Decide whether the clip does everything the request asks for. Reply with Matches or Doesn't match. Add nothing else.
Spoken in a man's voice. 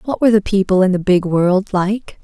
Doesn't match